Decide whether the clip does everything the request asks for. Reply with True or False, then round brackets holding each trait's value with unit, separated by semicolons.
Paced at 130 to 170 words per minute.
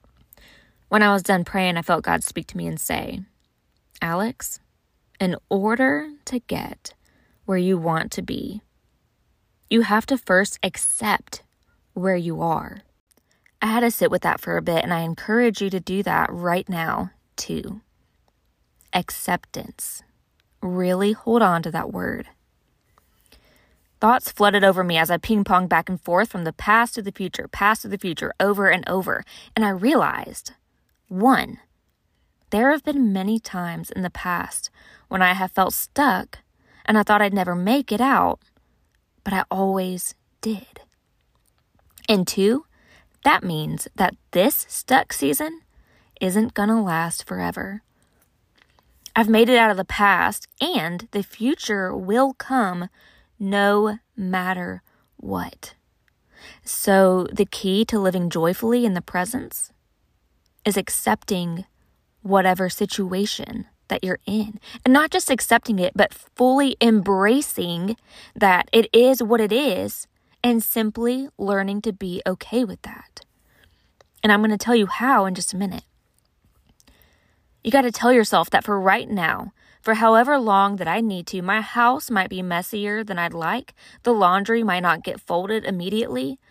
True (150 wpm)